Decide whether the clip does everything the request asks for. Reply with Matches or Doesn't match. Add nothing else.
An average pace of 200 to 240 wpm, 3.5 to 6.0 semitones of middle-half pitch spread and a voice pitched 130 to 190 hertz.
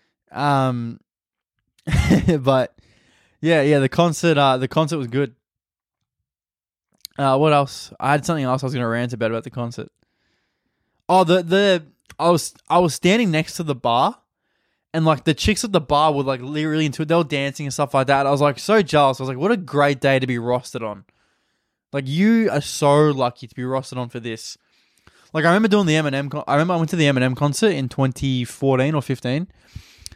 Matches